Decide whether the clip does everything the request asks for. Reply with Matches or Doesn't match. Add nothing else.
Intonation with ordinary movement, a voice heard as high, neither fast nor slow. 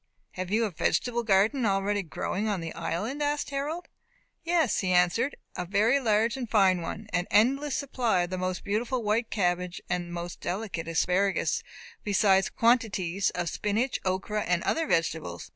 Matches